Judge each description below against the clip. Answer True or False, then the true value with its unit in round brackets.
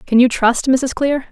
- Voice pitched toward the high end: True (255 Hz)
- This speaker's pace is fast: True (230 wpm)